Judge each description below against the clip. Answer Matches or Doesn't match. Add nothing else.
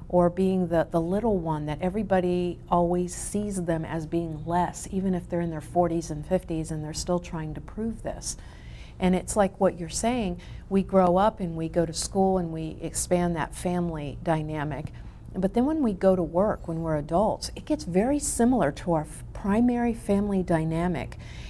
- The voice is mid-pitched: Matches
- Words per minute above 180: Matches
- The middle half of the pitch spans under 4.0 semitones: Matches